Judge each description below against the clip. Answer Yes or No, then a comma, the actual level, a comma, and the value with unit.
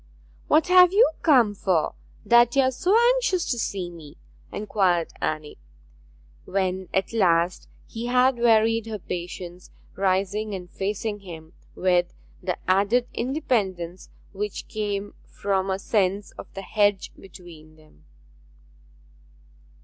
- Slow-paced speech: Yes, slow, 125 wpm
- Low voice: No, high, 195 Hz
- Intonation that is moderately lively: Yes, average, 4.1 semitones